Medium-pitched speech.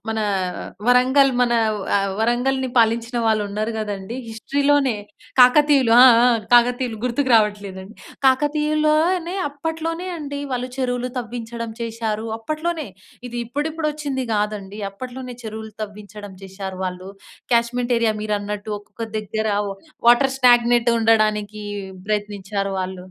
No: high, 235 Hz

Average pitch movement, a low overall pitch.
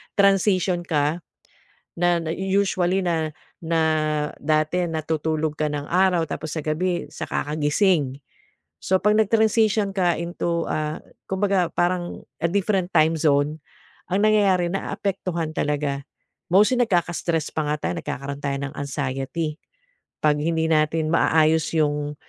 No: average, 3.5 semitones; medium, 165 Hz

